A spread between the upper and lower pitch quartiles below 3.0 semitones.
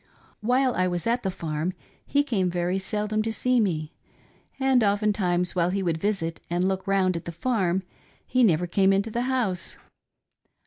No: average, 3.9 semitones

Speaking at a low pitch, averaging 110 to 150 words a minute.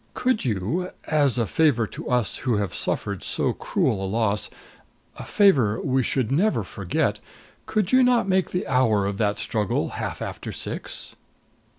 No: low, 125 Hz; average, 165 wpm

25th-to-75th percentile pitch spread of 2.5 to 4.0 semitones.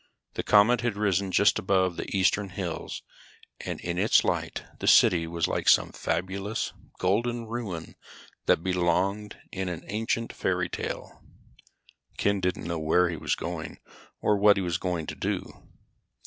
Yes: average, 2.8 semitones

